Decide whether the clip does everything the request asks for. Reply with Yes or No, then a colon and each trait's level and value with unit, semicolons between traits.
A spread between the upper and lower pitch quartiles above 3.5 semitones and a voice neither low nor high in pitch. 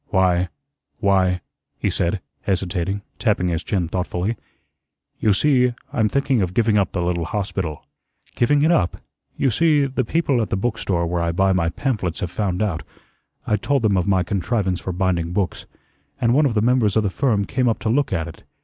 No: average, 4.8 semitones; low, 100 Hz